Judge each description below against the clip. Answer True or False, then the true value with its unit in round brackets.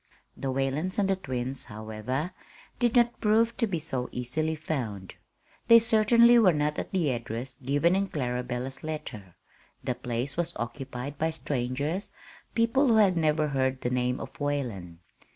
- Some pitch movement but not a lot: False (6.9 semitones)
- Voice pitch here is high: False (145 Hz)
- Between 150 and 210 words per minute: True (155 wpm)